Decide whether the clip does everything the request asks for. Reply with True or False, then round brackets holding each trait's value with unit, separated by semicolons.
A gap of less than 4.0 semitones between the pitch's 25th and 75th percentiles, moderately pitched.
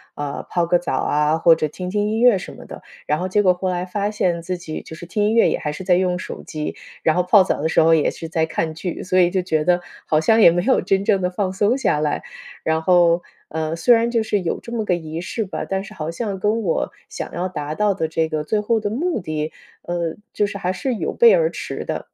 False (4.3 semitones; 180 Hz)